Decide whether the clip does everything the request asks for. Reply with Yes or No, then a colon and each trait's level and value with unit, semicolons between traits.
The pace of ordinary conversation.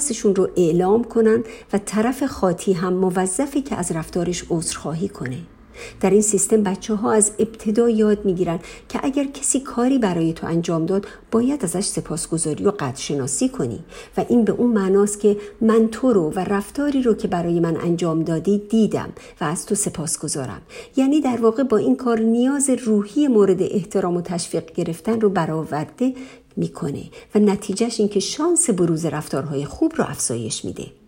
No: fast, 170 wpm